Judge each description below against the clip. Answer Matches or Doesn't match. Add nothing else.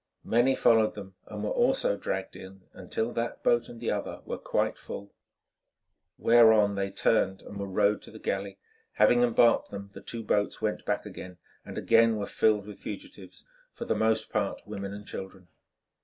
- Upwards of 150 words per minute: Matches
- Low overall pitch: Matches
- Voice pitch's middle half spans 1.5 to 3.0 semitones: Matches